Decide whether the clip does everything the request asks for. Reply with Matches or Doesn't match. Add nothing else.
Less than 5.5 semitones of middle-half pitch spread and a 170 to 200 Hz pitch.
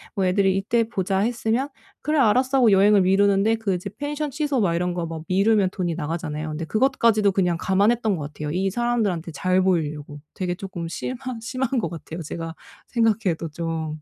Matches